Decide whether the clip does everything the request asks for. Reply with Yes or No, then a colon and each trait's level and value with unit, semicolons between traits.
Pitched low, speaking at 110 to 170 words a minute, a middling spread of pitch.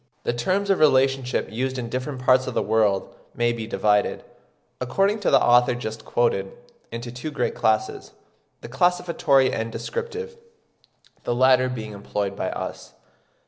Yes: low, 125 Hz; average, 150 wpm; average, 3.3 semitones